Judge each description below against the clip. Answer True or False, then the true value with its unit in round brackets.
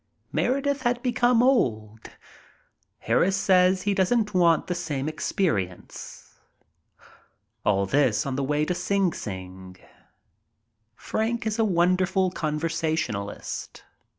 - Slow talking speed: True (110 wpm)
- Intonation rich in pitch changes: True (7.7 semitones)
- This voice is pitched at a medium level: True (175 Hz)